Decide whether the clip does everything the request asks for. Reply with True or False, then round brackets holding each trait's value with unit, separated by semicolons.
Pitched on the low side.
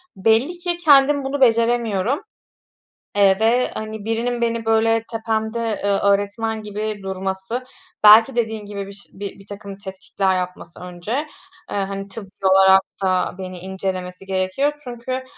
False (210 Hz)